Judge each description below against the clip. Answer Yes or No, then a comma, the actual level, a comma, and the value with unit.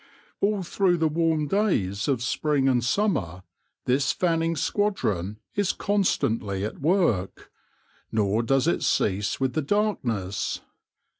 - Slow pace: Yes, slow, 125 wpm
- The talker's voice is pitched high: No, medium, 140 Hz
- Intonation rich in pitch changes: Yes, wide, 9.0 semitones